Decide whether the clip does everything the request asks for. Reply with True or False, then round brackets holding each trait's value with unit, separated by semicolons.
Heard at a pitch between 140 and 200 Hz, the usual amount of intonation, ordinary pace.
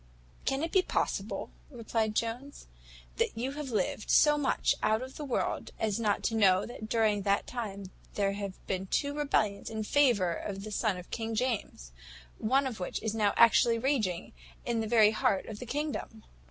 False (220 Hz; 3.9 semitones; 185 wpm)